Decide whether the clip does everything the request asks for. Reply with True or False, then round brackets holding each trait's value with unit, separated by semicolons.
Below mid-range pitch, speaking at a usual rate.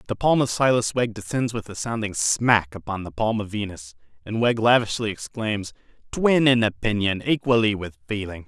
True (110 Hz; 175 wpm)